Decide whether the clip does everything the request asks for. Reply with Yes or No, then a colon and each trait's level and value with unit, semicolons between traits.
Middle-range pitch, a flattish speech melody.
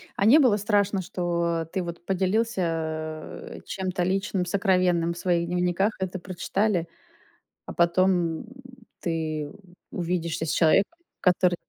Yes: medium, 180 Hz; narrow, 2.2 semitones